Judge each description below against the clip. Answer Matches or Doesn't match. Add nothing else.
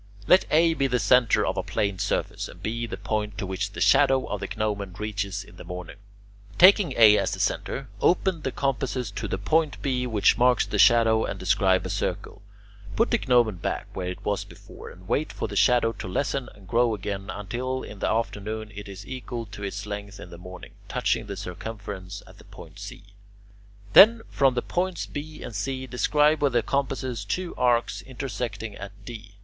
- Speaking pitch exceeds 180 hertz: Doesn't match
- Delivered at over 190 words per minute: Matches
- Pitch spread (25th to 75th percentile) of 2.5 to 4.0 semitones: Doesn't match